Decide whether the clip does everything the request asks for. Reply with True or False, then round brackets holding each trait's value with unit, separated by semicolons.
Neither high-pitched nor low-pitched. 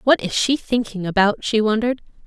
False (220 Hz)